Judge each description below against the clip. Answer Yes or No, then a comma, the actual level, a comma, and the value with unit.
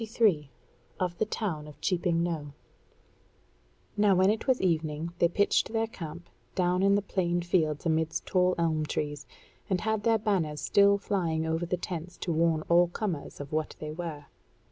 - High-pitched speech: No, medium, 175 Hz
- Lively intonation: No, average, 3.8 semitones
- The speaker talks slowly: No, average, 170 wpm